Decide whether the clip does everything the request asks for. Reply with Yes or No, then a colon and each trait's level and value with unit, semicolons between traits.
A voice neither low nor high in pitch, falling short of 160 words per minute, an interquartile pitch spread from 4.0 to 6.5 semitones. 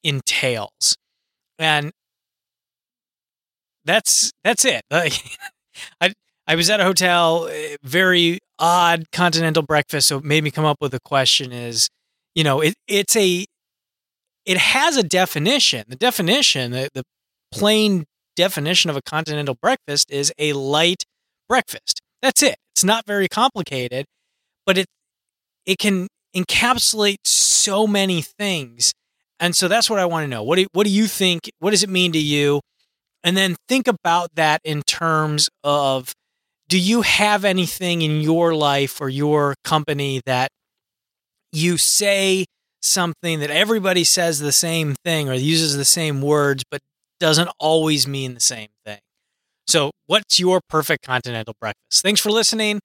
Yes: medium, 165 Hz; average, 150 wpm; average, 5.0 semitones